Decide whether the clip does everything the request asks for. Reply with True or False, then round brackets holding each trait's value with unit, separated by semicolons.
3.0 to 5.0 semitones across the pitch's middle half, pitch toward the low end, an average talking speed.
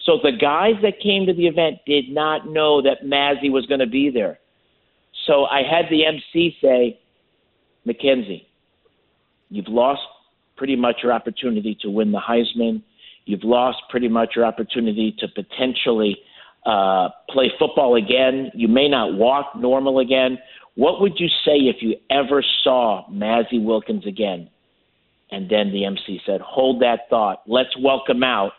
True (3.9 semitones; 130 Hz; 155 wpm)